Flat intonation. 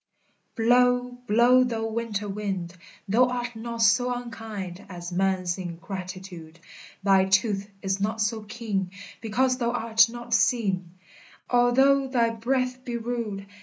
No: average, 3.9 semitones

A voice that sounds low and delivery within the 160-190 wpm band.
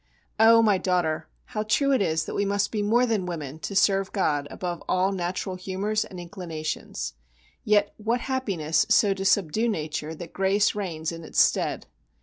No: high, 190 Hz; average, 175 wpm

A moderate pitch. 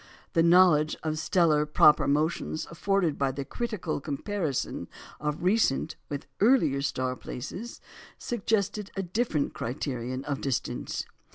Yes: medium, 155 Hz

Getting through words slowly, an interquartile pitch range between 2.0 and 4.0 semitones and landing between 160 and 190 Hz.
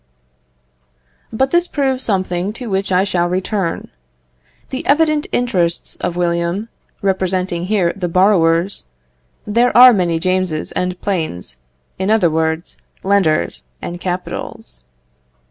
Yes: slow, 115 wpm; average, 3.5 semitones; medium, 185 Hz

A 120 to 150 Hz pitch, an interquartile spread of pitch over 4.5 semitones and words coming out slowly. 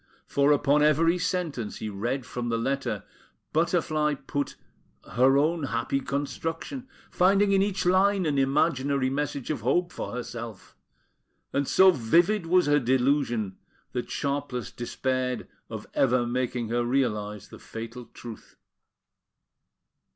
Yes: medium, 140 Hz; average, 5.1 semitones; slow, 130 wpm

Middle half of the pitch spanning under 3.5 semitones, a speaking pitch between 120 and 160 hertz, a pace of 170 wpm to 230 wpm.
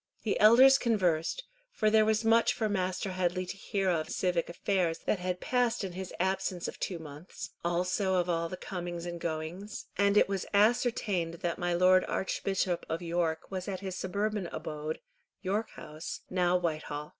No: average, 2.7 semitones; medium, 185 Hz; average, 175 wpm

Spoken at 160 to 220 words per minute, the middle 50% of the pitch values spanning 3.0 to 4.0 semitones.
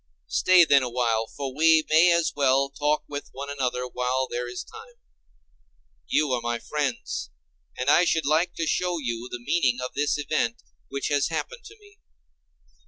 No: average, 170 wpm; average, 4.4 semitones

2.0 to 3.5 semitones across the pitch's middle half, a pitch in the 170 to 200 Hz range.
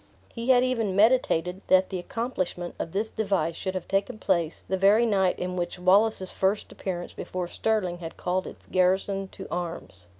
Yes: average, 2.9 semitones; high, 190 Hz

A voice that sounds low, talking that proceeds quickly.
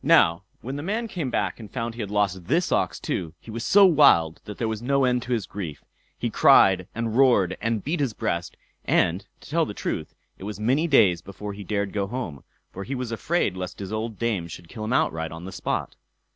Yes: low, 110 Hz; fast, 230 wpm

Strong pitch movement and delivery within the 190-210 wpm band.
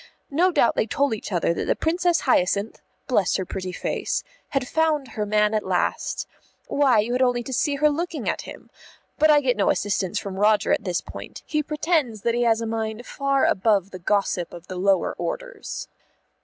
Yes: wide, 6.3 semitones; average, 200 wpm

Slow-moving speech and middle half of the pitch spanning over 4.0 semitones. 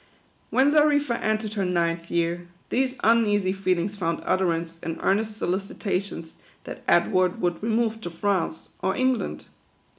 Yes: slow, 130 wpm; average, 4.4 semitones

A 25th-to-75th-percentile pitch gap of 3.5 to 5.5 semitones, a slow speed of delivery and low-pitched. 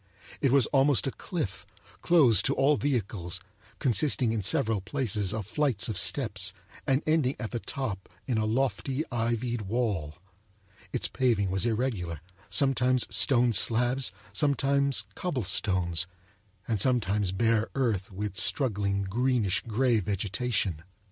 Yes: average, 5.1 semitones; slow, 130 wpm; low, 115 Hz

